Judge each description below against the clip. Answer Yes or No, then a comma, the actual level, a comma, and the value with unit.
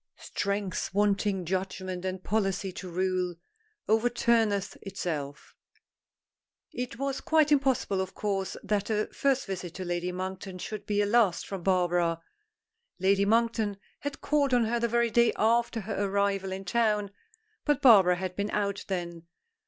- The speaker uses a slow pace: No, average, 145 wpm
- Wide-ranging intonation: No, average, 3.4 semitones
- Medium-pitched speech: No, high, 200 Hz